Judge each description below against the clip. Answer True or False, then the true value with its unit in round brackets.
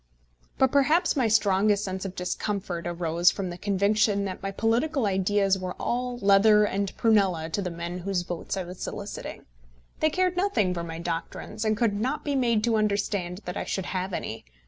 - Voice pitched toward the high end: True (200 Hz)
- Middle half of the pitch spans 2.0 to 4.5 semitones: True (3.5 semitones)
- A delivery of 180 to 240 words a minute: True (190 wpm)